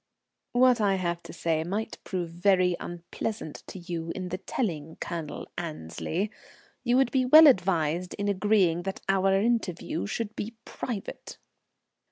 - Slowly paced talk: No, average, 145 wpm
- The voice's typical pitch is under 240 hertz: Yes, medium, 185 Hz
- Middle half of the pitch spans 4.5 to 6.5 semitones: No, average, 4.0 semitones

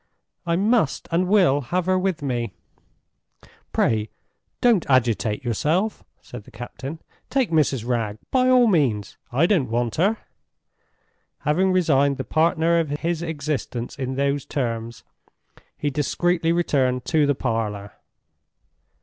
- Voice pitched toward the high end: No, medium, 145 Hz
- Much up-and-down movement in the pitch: Yes, wide, 6.0 semitones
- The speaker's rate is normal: No, slow, 130 wpm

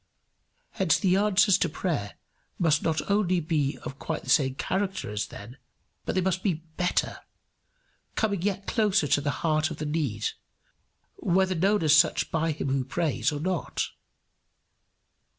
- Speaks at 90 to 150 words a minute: No, average, 160 wpm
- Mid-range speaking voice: Yes, medium, 165 Hz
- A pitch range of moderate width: Yes, average, 4.5 semitones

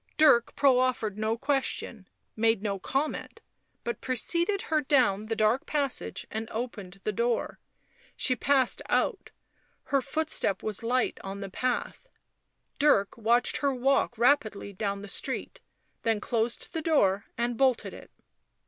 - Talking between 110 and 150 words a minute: Yes, average, 140 wpm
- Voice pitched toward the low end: No, high, 235 Hz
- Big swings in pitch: No, average, 4.1 semitones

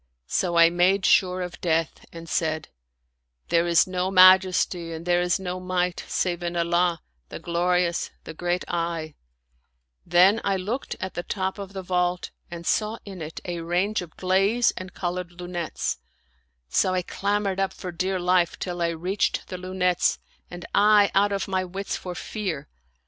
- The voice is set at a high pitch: No, medium, 180 Hz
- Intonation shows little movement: Yes, narrow, 1.7 semitones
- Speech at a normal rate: Yes, average, 180 wpm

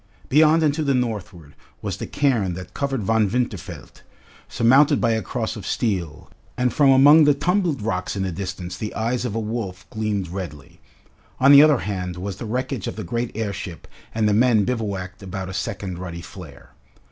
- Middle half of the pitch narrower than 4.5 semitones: No, wide, 5.4 semitones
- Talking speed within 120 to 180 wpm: No, average, 190 wpm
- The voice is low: Yes, low, 105 Hz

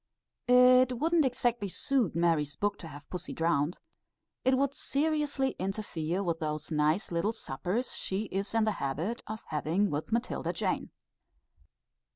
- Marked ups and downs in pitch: Yes, wide, 7.4 semitones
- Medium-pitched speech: No, high, 200 Hz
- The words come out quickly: No, average, 145 wpm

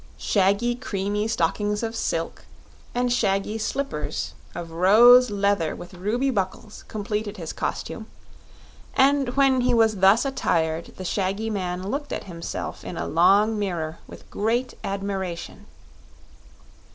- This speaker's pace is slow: Yes, slow, 125 wpm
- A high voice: Yes, high, 205 Hz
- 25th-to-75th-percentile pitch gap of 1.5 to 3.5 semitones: No, average, 4.1 semitones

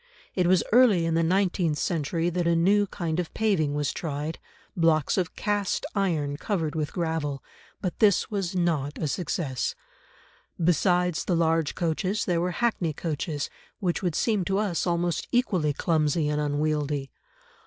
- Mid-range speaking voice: Yes, medium, 170 Hz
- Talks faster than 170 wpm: No, average, 155 wpm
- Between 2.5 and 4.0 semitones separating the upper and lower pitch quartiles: Yes, average, 3.3 semitones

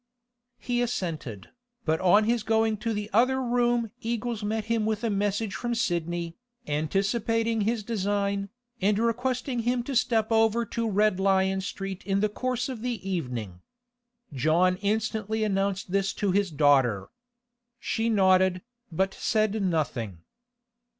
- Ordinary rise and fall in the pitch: Yes, average, 3.4 semitones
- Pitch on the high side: Yes, high, 205 Hz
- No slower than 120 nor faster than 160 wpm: Yes, average, 140 wpm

